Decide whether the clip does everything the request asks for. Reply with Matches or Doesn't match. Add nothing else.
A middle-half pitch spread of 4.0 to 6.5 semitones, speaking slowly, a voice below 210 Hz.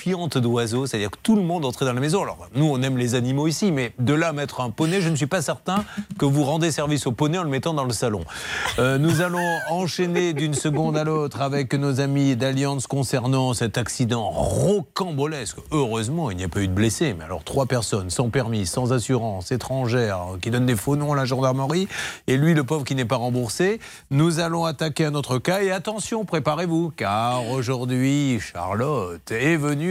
Doesn't match